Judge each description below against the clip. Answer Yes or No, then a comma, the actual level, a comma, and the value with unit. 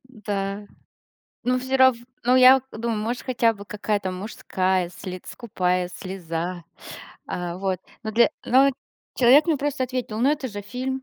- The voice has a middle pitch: No, high, 220 Hz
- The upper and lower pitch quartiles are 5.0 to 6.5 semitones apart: Yes, average, 5.3 semitones